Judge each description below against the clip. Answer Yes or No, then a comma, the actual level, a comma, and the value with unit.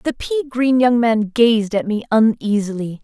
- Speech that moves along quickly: No, average, 180 wpm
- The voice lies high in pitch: Yes, high, 225 Hz